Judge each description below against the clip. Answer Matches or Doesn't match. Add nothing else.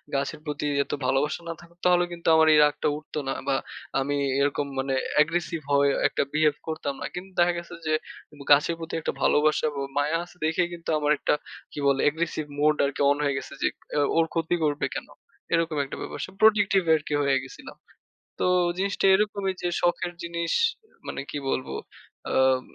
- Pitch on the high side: Doesn't match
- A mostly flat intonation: Doesn't match